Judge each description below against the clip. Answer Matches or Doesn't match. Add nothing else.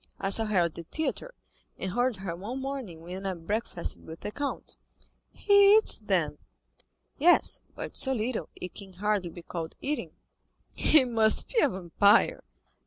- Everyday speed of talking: Matches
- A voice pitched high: Matches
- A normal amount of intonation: Doesn't match